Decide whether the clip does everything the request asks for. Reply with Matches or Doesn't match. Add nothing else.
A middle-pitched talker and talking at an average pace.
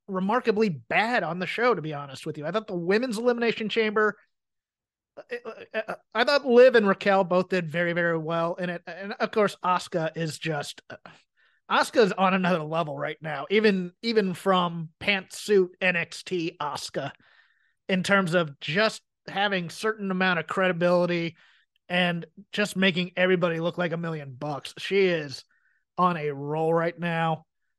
Matches